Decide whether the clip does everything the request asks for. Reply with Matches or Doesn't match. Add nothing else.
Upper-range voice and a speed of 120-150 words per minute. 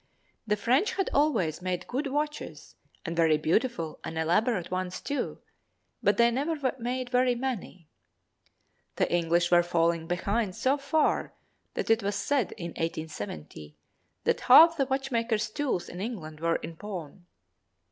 Matches